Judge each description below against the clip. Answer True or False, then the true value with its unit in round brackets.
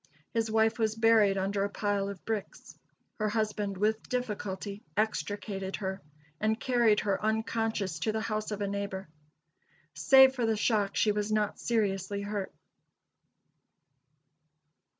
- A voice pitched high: True (210 Hz)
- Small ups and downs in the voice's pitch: True (1.8 semitones)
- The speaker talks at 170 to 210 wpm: False (135 wpm)